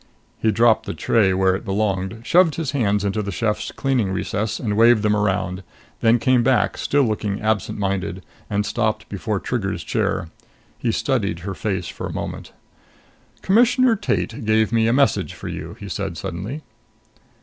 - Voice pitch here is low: Yes, low, 110 Hz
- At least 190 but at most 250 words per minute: No, average, 170 wpm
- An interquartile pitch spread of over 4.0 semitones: No, average, 3.5 semitones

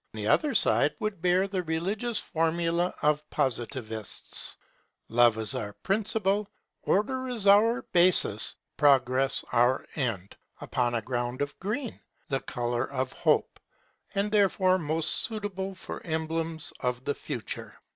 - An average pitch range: No, wide, 7.8 semitones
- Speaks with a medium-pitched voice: Yes, medium, 160 Hz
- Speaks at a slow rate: Yes, slow, 130 wpm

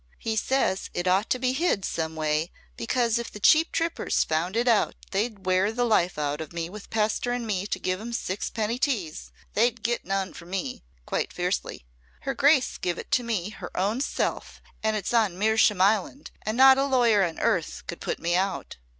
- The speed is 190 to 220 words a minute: Yes, average, 200 wpm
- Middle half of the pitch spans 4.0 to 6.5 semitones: Yes, average, 4.5 semitones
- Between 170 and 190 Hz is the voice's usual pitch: No, high, 210 Hz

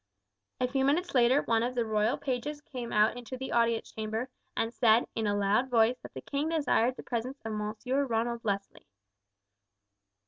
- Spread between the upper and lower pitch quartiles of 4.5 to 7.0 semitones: No, average, 2.8 semitones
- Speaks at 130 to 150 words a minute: No, average, 180 wpm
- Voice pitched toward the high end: Yes, high, 235 Hz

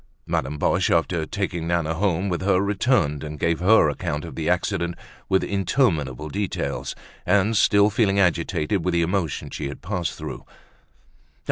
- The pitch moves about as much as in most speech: Yes, average, 4.0 semitones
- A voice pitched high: No, very low, 90 Hz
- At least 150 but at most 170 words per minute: Yes, average, 155 wpm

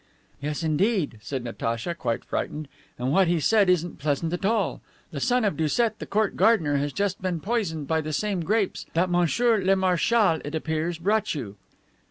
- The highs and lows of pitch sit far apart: No, average, 5.0 semitones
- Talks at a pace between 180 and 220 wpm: Yes, average, 185 wpm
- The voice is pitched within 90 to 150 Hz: No, medium, 175 Hz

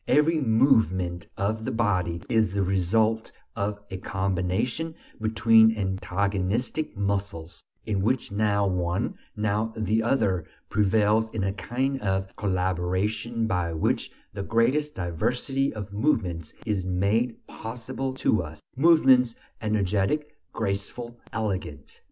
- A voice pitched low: Yes, low, 105 Hz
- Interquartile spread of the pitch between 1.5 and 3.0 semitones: No, average, 3.5 semitones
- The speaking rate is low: Yes, slow, 115 wpm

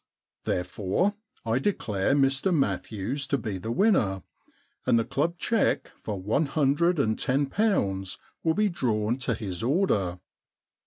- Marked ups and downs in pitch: Yes, wide, 7.9 semitones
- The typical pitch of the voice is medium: No, low, 130 Hz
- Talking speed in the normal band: Yes, average, 145 wpm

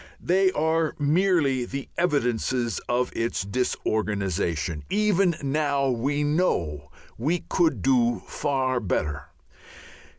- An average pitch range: No, wide, 5.8 semitones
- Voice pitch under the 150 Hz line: Yes, low, 135 Hz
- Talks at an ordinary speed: No, slow, 100 wpm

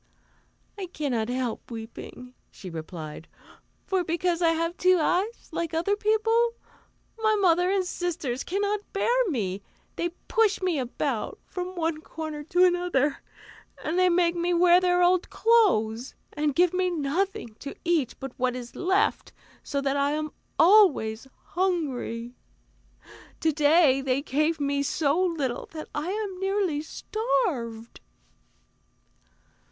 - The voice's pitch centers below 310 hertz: No, very high, 330 Hz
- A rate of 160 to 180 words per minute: No, slow, 135 wpm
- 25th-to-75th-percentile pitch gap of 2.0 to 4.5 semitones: No, average, 5.3 semitones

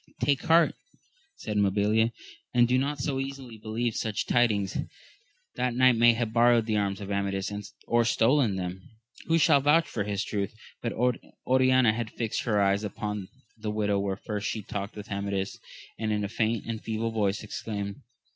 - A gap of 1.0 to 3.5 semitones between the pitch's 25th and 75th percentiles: Yes, average, 3.0 semitones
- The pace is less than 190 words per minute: Yes, average, 175 wpm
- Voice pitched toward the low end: Yes, low, 110 Hz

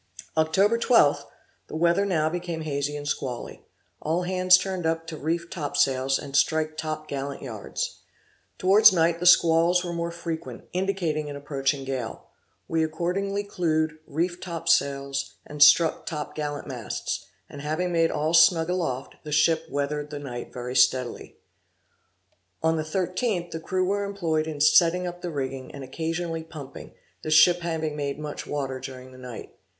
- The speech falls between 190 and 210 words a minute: No, average, 165 wpm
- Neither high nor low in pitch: Yes, medium, 160 Hz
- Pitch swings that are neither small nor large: Yes, average, 3.3 semitones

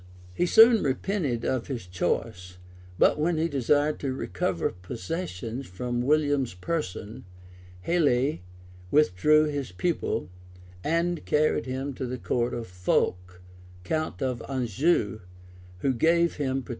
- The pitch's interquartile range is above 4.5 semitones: Yes, average, 5.3 semitones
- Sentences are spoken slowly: Yes, slow, 130 wpm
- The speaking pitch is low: Yes, low, 130 Hz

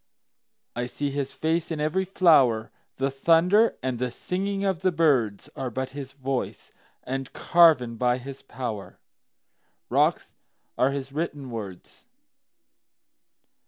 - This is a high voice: No, low, 135 Hz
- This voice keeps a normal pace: No, slow, 110 wpm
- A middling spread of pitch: Yes, average, 4.7 semitones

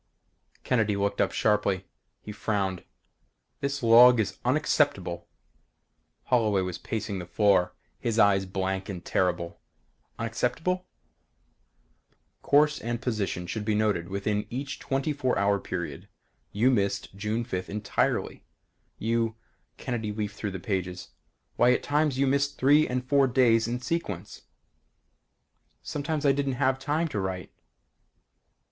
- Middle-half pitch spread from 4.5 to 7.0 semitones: Yes, average, 5.1 semitones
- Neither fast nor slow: No, slow, 130 wpm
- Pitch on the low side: Yes, low, 110 Hz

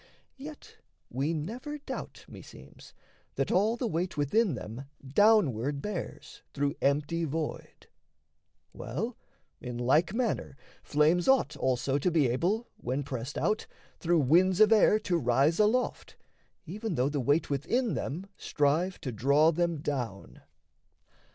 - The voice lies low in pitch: No, medium, 155 Hz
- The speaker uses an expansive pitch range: Yes, wide, 6.8 semitones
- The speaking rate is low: Yes, slow, 130 wpm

